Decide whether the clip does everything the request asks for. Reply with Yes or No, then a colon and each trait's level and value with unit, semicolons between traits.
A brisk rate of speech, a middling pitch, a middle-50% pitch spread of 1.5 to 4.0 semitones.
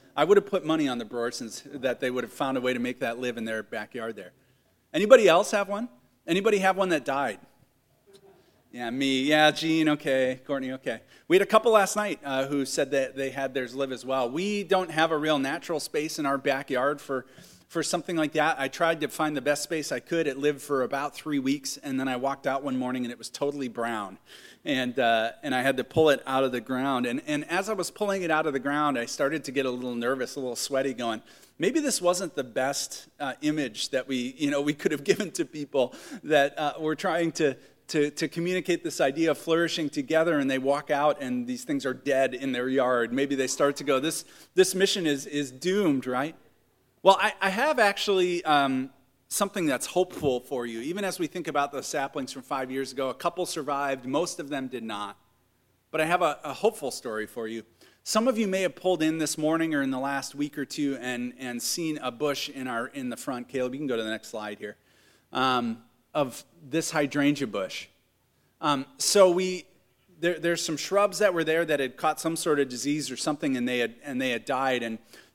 No: fast, 230 wpm; medium, 145 Hz; average, 4.4 semitones